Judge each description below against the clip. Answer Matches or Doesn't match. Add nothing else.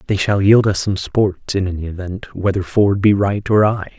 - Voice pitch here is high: Doesn't match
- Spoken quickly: Matches